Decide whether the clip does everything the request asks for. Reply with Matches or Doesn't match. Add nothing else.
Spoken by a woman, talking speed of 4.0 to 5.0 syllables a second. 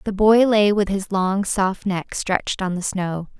Matches